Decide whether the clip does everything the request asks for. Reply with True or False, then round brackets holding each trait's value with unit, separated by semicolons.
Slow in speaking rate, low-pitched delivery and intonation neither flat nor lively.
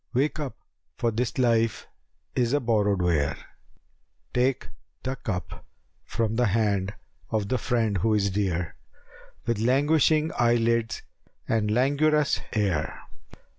True (130 wpm; 115 Hz; 3.7 semitones)